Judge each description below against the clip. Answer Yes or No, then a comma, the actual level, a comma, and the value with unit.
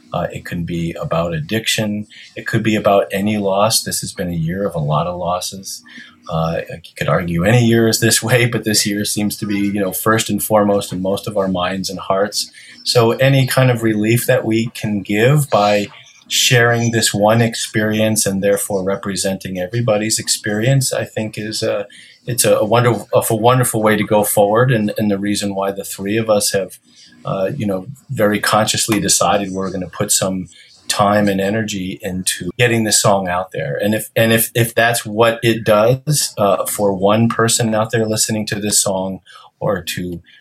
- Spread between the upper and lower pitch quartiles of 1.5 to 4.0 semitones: Yes, narrow, 2.5 semitones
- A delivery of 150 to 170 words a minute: No, average, 195 wpm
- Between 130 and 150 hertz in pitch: No, low, 105 Hz